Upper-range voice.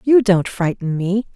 Yes: high, 200 Hz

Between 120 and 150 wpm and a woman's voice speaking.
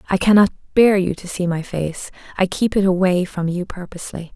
No: fast, 205 wpm; female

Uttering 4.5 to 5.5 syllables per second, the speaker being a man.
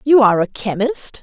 No: 5.3 syllables/s; female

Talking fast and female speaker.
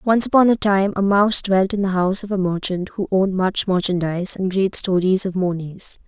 Yes: fast, 215 wpm; female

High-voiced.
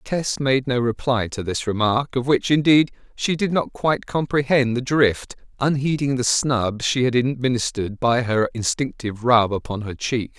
No: low, 125 Hz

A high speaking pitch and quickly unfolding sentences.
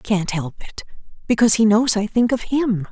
Yes: high, 215 Hz; fast, 225 wpm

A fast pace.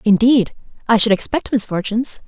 No: slow, 130 wpm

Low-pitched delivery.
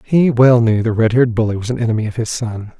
Yes: low, 115 Hz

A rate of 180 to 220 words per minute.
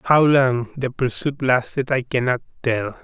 No: average, 160 wpm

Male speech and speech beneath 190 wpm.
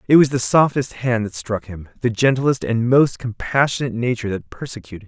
No: male; average, 200 wpm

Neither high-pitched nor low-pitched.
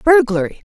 No: very high, 260 Hz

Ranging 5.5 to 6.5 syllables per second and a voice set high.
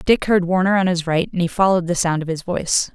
No: 6.4 syllables/s; medium, 175 Hz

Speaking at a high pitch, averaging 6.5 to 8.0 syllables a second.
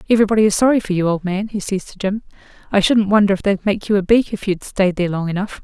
Yes: high, 200 Hz; 6.9 syllables/s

